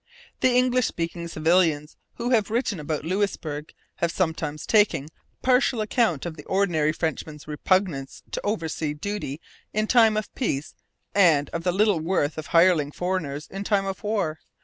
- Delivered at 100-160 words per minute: Yes, average, 150 wpm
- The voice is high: No, medium, 175 Hz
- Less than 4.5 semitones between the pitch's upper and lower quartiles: No, average, 5.1 semitones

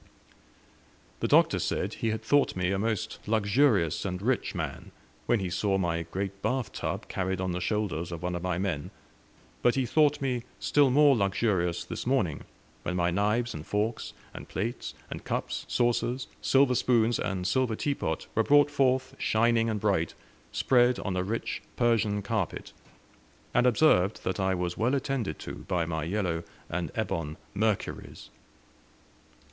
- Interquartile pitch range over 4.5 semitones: Yes, average, 5.1 semitones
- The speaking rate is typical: Yes, average, 160 wpm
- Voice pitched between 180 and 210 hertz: No, low, 105 Hz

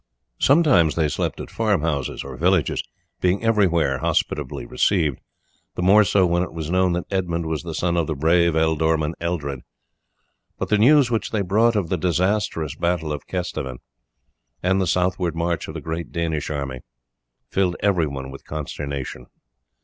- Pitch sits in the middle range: No, very low, 85 Hz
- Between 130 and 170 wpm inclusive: Yes, average, 165 wpm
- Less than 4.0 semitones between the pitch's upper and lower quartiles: Yes, average, 3.3 semitones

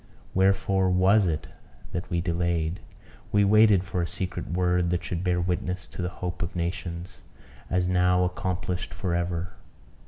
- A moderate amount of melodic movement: No, narrow, 1.2 semitones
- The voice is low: Yes, very low, 90 Hz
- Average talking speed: Yes, average, 155 wpm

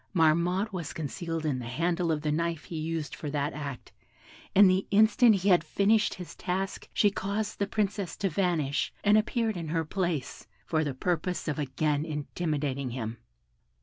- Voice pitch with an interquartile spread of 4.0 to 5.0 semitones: Yes, average, 4.5 semitones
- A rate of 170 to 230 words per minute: Yes, average, 175 wpm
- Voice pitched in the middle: Yes, medium, 165 Hz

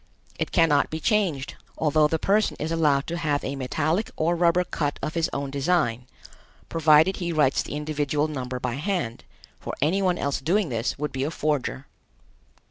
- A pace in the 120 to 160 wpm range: No, average, 180 wpm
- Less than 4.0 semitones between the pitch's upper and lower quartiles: Yes, average, 3.3 semitones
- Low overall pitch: No, medium, 150 Hz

